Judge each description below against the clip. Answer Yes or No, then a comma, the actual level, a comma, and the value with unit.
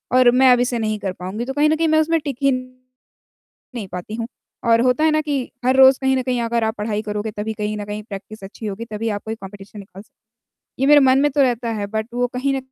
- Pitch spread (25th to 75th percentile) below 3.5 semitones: No, average, 3.8 semitones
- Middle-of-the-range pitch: No, high, 235 Hz